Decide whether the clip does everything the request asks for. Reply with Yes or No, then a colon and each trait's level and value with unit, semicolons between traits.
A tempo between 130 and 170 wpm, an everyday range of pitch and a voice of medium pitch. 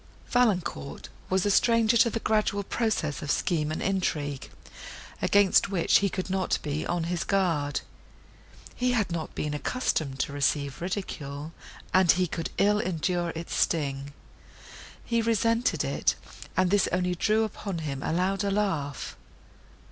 Yes: average, 145 wpm; average, 5.0 semitones; medium, 180 Hz